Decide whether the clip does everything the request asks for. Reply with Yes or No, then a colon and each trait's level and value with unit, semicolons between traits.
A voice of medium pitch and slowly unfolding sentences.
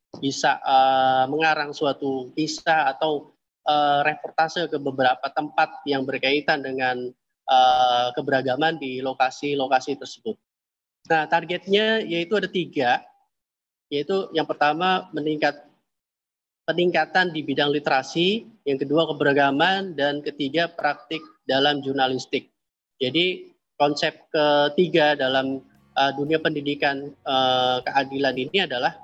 No: medium, 145 Hz; average, 105 wpm